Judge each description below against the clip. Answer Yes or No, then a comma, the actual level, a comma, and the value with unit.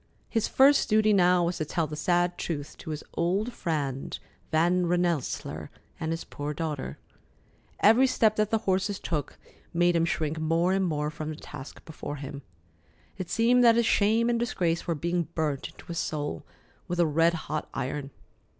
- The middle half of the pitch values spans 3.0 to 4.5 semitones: Yes, average, 4.1 semitones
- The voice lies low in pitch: No, medium, 170 Hz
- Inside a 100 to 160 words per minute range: No, average, 175 wpm